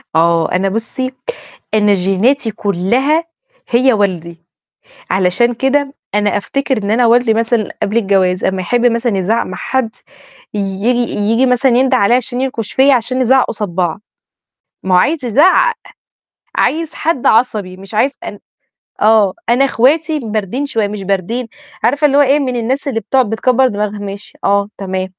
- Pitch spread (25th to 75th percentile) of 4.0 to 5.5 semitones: Yes, average, 4.5 semitones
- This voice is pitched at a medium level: No, high, 225 Hz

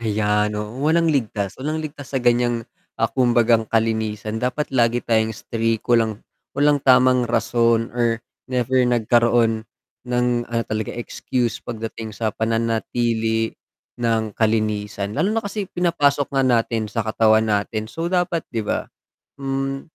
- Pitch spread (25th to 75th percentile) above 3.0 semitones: No, average, 2.7 semitones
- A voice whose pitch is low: Yes, low, 115 Hz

